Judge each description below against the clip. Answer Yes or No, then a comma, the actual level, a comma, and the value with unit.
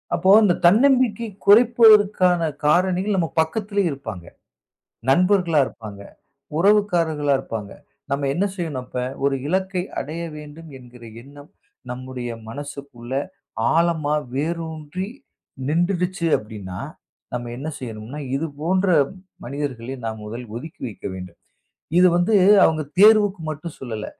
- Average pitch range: No, wide, 6.4 semitones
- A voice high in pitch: No, medium, 155 Hz